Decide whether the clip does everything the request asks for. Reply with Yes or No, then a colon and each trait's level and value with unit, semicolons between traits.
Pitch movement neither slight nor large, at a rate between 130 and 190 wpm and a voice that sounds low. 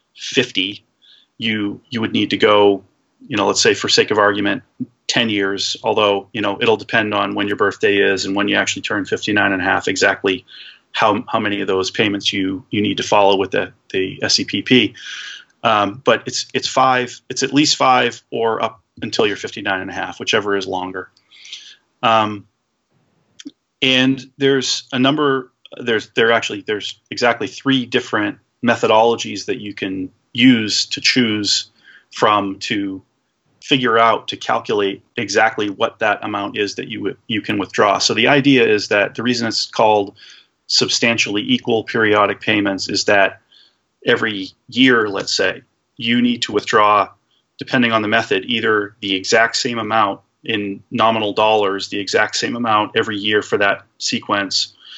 Yes: average, 3.5 semitones; average, 165 wpm; low, 110 Hz